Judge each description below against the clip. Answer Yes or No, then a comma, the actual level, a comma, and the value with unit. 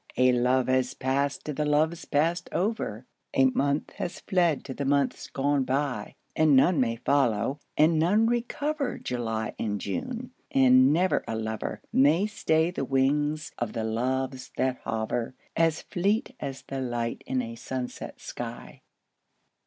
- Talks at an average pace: Yes, average, 155 wpm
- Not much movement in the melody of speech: No, average, 4.2 semitones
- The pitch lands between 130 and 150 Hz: Yes, low, 135 Hz